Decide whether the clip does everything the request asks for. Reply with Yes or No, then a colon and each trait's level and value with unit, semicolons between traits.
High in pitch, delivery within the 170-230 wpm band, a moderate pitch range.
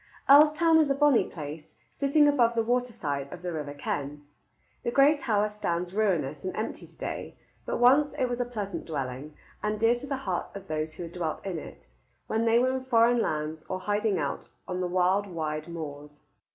No: high, 200 Hz; average, 200 wpm; wide, 7.5 semitones